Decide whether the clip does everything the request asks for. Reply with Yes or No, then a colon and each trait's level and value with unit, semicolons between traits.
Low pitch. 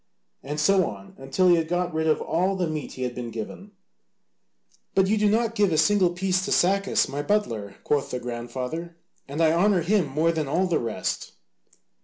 No: medium, 165 Hz